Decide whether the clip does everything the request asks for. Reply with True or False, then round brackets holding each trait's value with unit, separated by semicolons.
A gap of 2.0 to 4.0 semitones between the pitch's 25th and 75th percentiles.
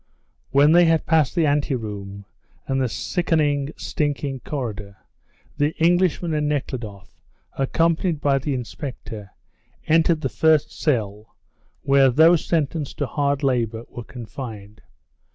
False (4.9 semitones)